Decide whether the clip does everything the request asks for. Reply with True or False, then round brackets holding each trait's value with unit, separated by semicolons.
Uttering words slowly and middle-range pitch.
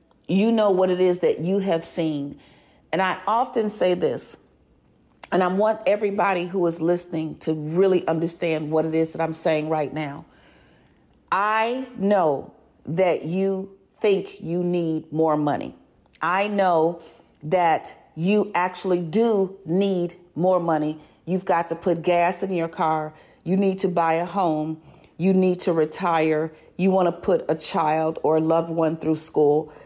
False (160 wpm; 175 Hz)